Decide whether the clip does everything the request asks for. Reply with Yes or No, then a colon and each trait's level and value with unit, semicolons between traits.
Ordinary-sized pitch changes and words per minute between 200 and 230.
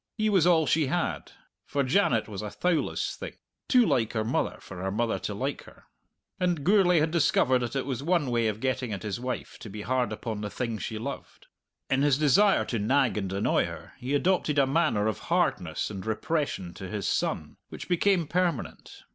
No: wide, 7.0 semitones; fast, 205 wpm